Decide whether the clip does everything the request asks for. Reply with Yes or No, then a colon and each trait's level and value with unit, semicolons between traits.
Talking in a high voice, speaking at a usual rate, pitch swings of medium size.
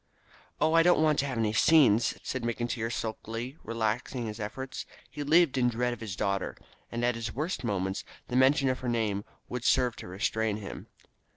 No: low, 120 Hz; average, 190 wpm; average, 3.2 semitones